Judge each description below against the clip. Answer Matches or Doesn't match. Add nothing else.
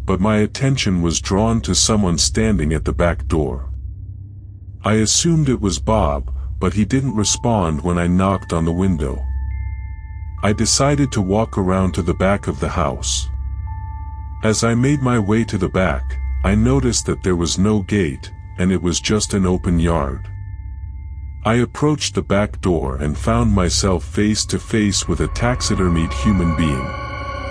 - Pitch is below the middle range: Matches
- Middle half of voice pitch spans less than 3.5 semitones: Doesn't match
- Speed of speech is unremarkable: Matches